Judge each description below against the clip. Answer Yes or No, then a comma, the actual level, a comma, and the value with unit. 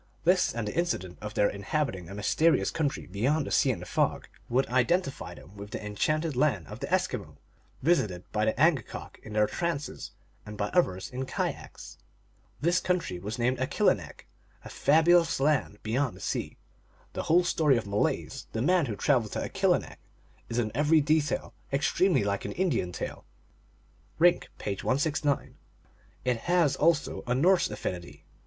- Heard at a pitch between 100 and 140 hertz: Yes, low, 135 Hz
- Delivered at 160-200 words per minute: Yes, average, 170 wpm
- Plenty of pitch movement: Yes, wide, 7.2 semitones